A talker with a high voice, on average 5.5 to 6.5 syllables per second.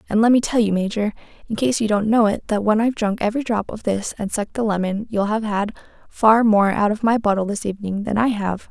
Yes: high, 215 Hz; 6.1 syllables/s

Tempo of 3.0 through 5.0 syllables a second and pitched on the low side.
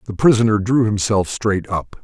Yes: 4.9 syllables/s; low, 105 Hz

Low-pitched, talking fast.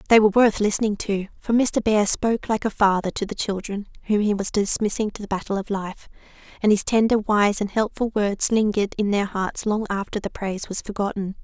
No: high, 205 Hz; fast, 215 wpm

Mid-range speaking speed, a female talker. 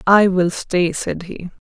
Yes: average, 180 wpm; female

